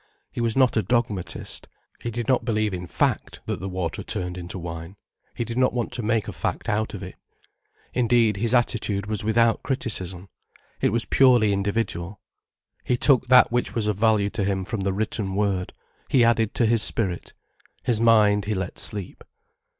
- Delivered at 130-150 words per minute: No, average, 185 wpm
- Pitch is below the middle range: Yes, low, 110 Hz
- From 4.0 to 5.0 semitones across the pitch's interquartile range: No, average, 3.3 semitones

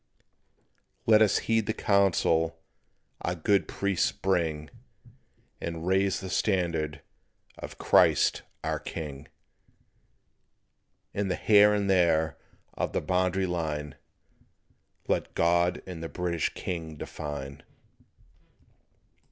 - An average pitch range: Yes, average, 3.3 semitones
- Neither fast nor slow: No, slow, 105 wpm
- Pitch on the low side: Yes, very low, 90 Hz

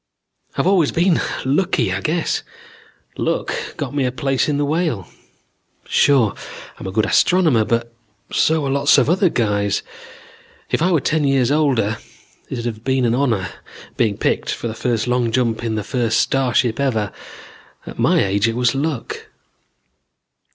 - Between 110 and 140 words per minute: No, average, 165 wpm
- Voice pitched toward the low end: Yes, low, 125 Hz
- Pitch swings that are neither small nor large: Yes, average, 4.3 semitones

